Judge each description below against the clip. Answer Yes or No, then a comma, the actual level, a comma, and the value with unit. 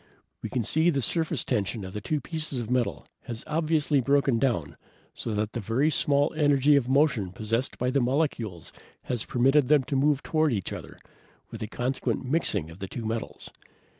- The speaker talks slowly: No, average, 185 wpm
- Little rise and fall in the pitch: No, average, 4.6 semitones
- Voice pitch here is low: Yes, low, 130 Hz